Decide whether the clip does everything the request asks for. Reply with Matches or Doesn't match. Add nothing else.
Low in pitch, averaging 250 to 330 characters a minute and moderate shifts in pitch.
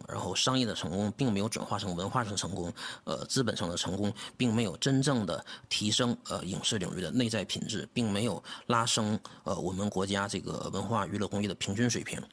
Matches